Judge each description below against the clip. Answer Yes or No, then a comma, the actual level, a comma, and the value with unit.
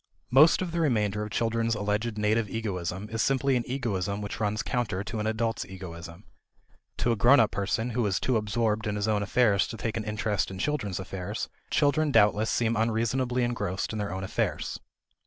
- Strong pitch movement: No, narrow, 2.6 semitones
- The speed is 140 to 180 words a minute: No, average, 195 wpm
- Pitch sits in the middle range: No, low, 110 Hz